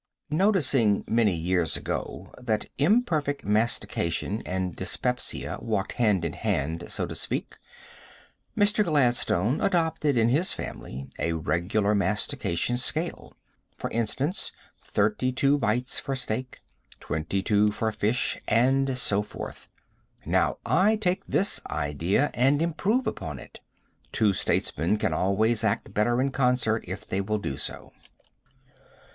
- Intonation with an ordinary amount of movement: No, wide, 6.1 semitones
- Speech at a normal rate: No, slow, 130 wpm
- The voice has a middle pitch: No, low, 115 Hz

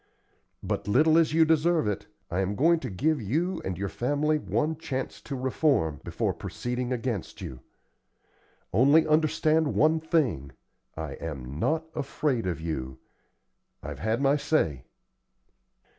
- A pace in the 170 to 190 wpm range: No, average, 140 wpm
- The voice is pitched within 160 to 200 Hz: No, low, 130 Hz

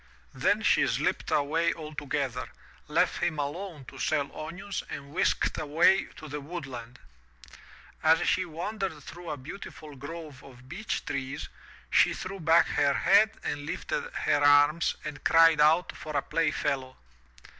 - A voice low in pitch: No, medium, 155 Hz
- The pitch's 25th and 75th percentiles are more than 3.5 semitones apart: No, average, 3.2 semitones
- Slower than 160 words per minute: Yes, average, 145 wpm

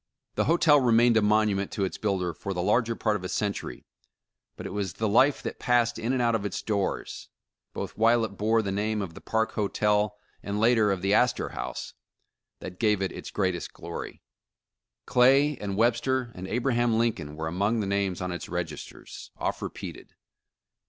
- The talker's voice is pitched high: No, low, 105 Hz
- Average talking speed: Yes, average, 185 wpm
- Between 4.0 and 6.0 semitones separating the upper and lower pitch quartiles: No, average, 3.1 semitones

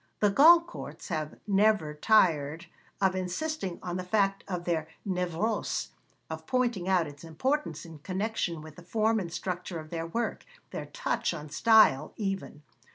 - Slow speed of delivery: No, average, 155 wpm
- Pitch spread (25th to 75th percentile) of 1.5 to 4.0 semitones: No, average, 4.9 semitones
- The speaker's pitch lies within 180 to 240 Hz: Yes, medium, 185 Hz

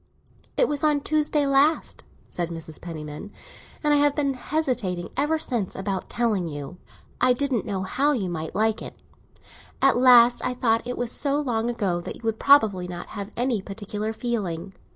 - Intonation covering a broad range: Yes, wide, 6.6 semitones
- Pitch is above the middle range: Yes, high, 230 Hz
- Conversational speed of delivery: Yes, average, 180 wpm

